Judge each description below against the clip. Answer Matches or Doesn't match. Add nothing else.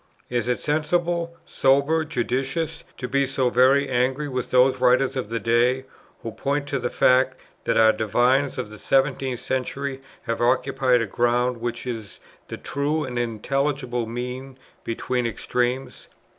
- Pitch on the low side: Matches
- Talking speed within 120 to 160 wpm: Matches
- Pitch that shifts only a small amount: Matches